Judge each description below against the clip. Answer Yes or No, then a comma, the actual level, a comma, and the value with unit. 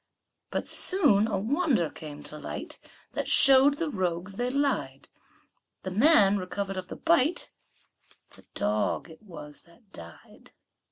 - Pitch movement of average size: No, wide, 8.4 semitones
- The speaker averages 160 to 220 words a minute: No, slow, 135 wpm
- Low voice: No, high, 195 Hz